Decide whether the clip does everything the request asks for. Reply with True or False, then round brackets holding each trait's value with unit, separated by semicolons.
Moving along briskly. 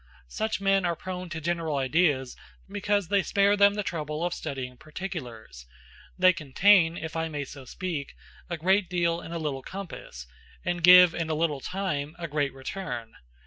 False (175 wpm)